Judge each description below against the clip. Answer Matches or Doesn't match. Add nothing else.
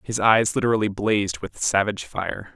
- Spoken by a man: Matches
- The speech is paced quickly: Doesn't match